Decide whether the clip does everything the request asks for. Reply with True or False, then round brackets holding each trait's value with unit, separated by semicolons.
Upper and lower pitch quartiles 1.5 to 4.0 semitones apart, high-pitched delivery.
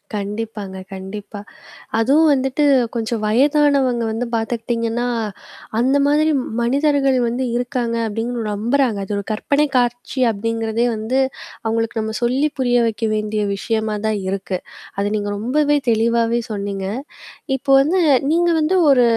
True (3.5 semitones; 230 Hz)